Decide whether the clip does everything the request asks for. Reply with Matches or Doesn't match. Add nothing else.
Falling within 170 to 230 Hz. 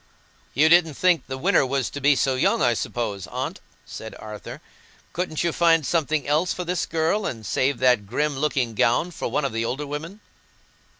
Doesn't match